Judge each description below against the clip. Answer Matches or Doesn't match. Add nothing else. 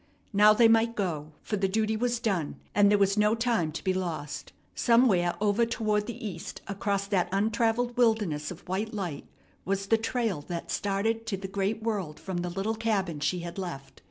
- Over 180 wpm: Matches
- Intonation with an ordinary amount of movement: Matches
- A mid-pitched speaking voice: Doesn't match